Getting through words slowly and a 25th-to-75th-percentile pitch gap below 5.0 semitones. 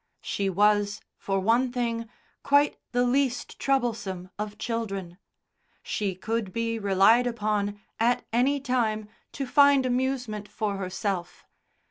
Yes: slow, 120 wpm; average, 3.5 semitones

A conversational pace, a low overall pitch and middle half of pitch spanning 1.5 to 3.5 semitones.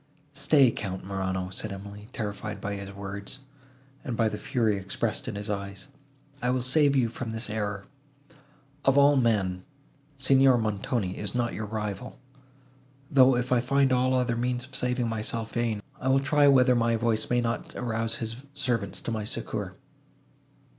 No: average, 165 wpm; low, 115 Hz; average, 4.0 semitones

